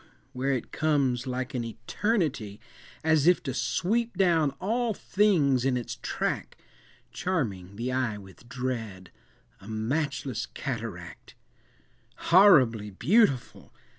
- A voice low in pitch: Yes, low, 130 Hz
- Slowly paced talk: Yes, slow, 105 wpm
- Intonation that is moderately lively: No, wide, 5.7 semitones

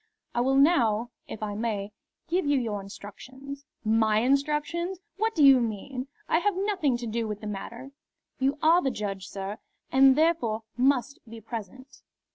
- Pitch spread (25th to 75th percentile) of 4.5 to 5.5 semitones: Yes, average, 4.8 semitones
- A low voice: No, very high, 255 Hz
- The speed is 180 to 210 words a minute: No, average, 165 wpm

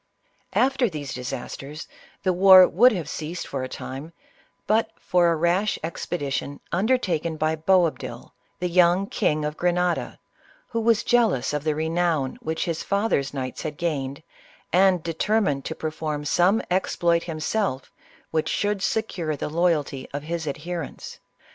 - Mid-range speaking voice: Yes, medium, 170 Hz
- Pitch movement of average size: Yes, average, 3.7 semitones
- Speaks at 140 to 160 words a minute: Yes, average, 150 wpm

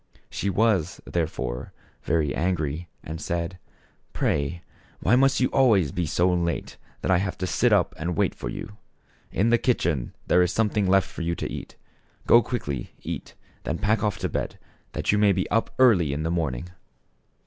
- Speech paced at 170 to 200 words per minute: Yes, average, 190 wpm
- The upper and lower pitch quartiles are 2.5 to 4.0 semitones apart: No, average, 4.5 semitones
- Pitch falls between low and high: No, very low, 90 Hz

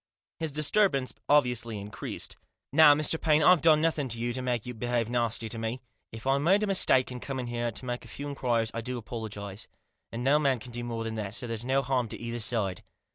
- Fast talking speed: Yes, fast, 235 wpm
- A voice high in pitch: No, low, 125 Hz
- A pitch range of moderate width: Yes, average, 3.5 semitones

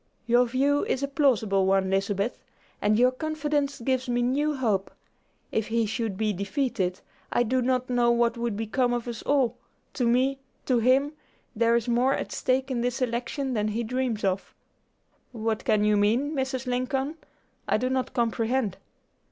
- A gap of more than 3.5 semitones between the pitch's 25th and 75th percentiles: No, average, 3.0 semitones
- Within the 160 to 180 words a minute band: Yes, average, 170 wpm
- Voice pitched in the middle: No, high, 245 Hz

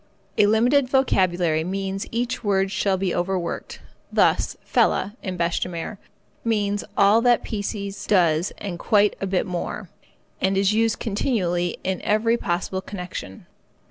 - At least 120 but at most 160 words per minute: Yes, average, 145 wpm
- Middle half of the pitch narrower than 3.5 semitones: Yes, average, 3.0 semitones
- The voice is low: No, high, 195 Hz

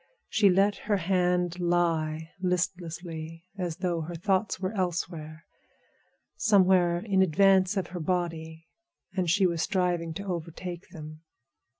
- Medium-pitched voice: Yes, medium, 175 Hz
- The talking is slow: Yes, slow, 120 wpm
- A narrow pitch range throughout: Yes, narrow, 2.3 semitones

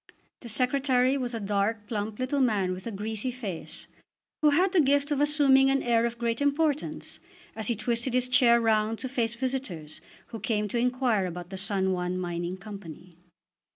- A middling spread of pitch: Yes, average, 4.6 semitones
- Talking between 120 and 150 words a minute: No, average, 185 wpm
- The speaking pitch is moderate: No, high, 235 Hz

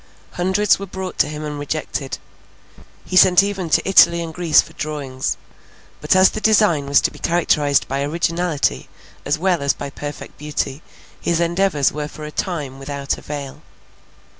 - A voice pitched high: No, medium, 155 Hz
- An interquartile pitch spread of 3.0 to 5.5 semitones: Yes, average, 3.9 semitones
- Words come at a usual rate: Yes, average, 165 wpm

